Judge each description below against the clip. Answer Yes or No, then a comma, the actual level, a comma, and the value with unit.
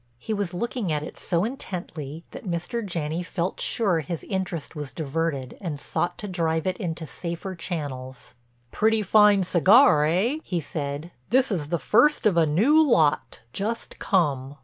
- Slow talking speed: No, average, 165 wpm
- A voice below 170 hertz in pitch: No, medium, 175 Hz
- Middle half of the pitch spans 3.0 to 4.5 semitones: No, average, 4.9 semitones